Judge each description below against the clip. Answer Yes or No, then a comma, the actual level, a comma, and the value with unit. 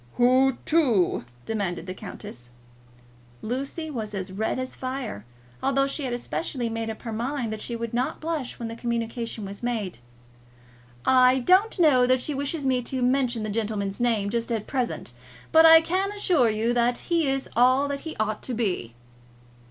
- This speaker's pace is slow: No, average, 175 wpm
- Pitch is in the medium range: No, high, 245 Hz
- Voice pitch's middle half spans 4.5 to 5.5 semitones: No, average, 3.7 semitones